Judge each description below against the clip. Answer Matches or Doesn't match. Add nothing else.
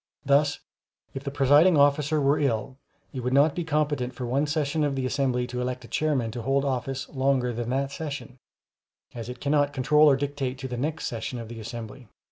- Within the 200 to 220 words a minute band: Matches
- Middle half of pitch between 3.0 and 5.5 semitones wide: Doesn't match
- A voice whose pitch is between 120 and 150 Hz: Matches